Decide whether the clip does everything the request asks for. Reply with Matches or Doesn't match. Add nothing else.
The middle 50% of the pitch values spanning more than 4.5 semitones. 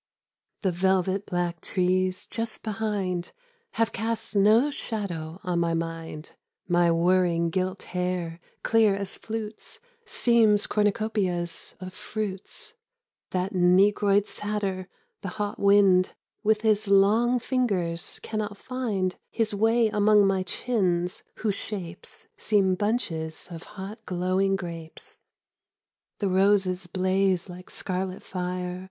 Doesn't match